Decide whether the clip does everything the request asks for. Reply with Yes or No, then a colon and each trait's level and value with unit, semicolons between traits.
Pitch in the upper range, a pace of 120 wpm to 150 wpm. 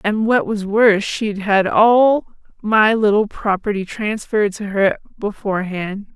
Yes: high, 210 Hz; slow, 135 wpm